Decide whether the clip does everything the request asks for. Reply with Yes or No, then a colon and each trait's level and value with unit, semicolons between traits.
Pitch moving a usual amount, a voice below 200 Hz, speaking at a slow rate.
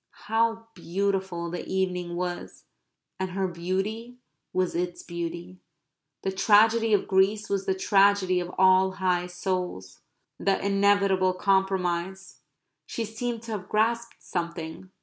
No: narrow, 2.2 semitones; high, 190 Hz; slow, 125 wpm